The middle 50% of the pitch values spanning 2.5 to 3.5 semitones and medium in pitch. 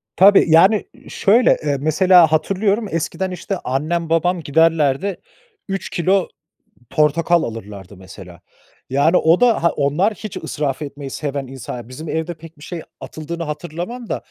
No: average, 4.4 semitones; medium, 160 Hz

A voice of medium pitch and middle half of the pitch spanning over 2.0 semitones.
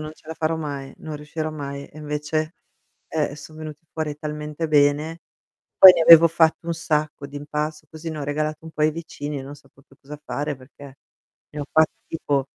No: medium, 150 Hz; narrow, 1.5 semitones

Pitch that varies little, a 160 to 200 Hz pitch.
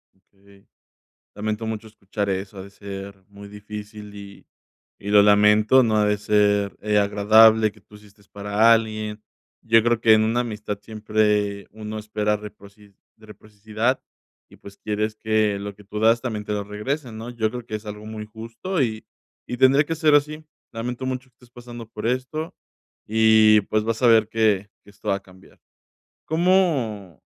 No: narrow, 1.7 semitones; low, 110 Hz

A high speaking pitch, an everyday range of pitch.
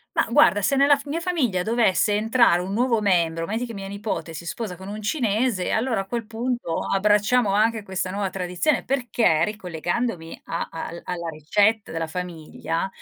Yes: high, 205 Hz; average, 4.6 semitones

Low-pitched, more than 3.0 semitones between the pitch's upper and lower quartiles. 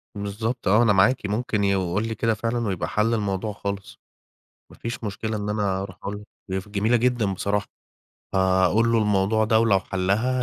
No: low, 105 Hz; narrow, 2.6 semitones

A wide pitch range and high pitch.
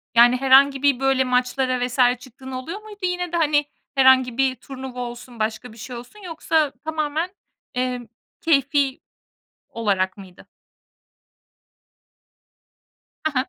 No: average, 2.8 semitones; very high, 260 Hz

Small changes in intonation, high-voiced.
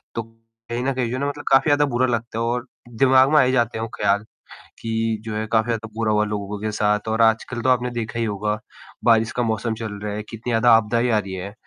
No: narrow, 2.1 semitones; low, 115 Hz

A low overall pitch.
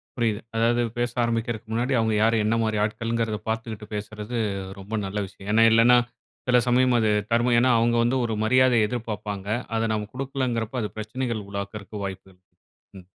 Yes: low, 115 Hz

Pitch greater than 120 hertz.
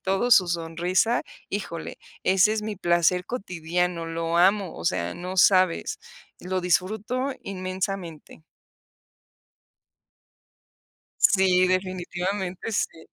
Yes: medium, 185 Hz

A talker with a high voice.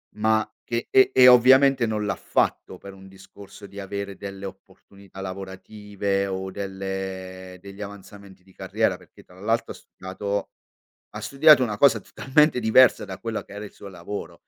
No: low, 100 Hz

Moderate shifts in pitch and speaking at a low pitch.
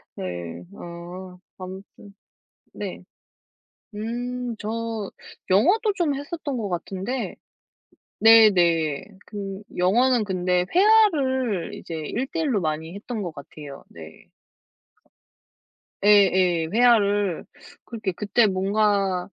No: average, 5.0 semitones; high, 205 Hz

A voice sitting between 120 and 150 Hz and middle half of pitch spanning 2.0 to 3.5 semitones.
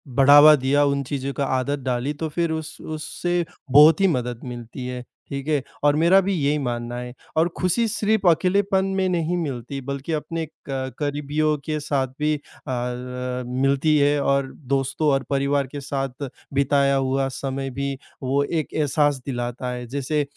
Yes: medium, 140 Hz; average, 2.7 semitones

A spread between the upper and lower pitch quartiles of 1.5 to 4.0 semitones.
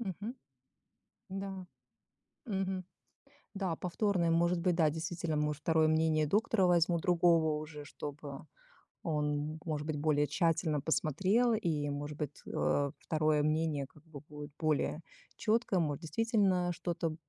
Yes: average, 3.3 semitones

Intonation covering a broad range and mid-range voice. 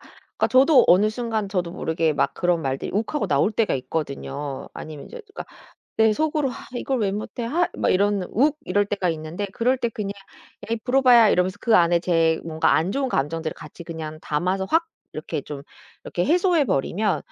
No: wide, 6.6 semitones; high, 195 Hz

